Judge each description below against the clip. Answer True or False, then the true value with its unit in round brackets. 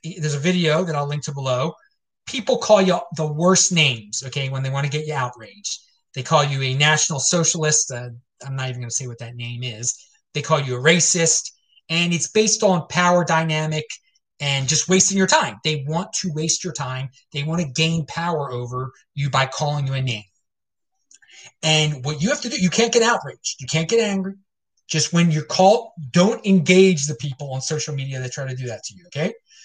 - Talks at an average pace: False (215 wpm)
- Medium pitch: True (155 Hz)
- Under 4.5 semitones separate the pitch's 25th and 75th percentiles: False (4.9 semitones)